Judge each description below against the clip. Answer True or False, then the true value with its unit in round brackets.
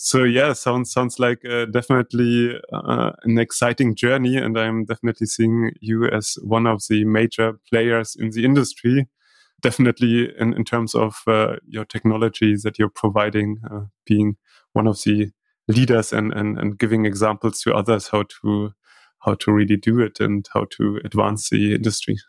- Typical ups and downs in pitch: False (2.1 semitones)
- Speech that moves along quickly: False (165 wpm)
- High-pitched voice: False (110 Hz)